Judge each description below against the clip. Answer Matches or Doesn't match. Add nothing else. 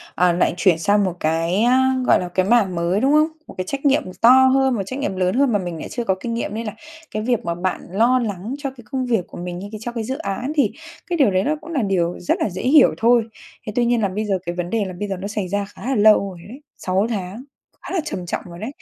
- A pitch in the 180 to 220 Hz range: Matches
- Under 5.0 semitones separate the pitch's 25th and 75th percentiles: Doesn't match